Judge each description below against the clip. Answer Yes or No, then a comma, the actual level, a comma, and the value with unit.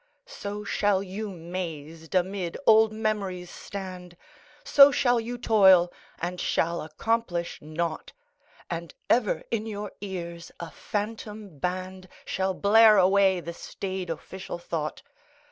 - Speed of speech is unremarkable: No, slow, 120 wpm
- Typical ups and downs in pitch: Yes, average, 3.5 semitones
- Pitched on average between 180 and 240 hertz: Yes, high, 190 Hz